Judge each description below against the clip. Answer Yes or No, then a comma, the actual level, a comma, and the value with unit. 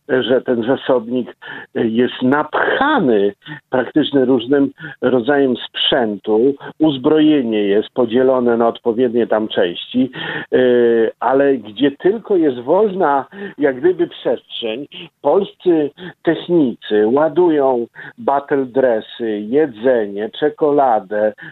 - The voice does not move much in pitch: No, average, 4.2 semitones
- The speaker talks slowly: Yes, slow, 85 wpm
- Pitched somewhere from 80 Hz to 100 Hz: No, low, 135 Hz